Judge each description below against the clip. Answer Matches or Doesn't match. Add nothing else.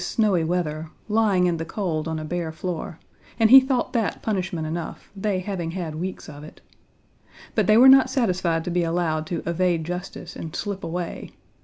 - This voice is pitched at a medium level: Matches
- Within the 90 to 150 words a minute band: Doesn't match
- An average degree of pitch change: Matches